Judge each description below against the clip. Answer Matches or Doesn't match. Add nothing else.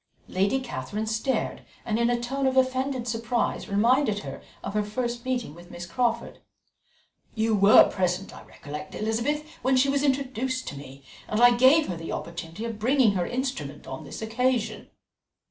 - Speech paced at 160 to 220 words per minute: Matches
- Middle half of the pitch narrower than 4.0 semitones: Doesn't match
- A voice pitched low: Doesn't match